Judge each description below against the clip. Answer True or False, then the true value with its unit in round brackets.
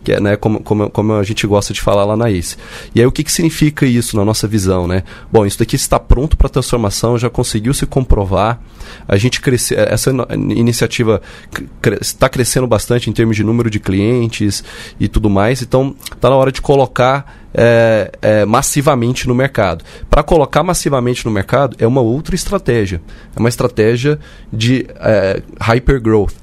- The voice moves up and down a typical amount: True (3.5 semitones)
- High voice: False (115 Hz)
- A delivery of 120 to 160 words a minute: False (185 wpm)